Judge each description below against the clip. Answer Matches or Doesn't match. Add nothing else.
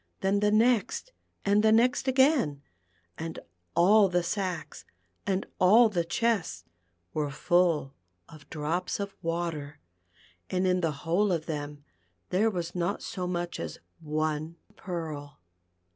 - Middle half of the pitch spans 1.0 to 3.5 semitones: Doesn't match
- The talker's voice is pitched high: Doesn't match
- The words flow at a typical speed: Doesn't match